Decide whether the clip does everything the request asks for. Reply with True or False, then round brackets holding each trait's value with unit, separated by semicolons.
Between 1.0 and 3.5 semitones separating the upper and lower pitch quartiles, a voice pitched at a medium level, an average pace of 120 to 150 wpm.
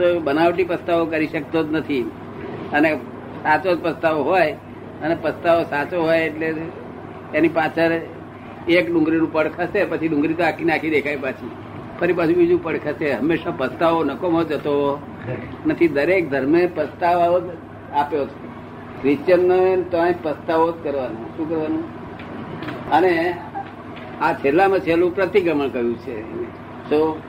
True (2.8 semitones; 165 Hz; 135 wpm)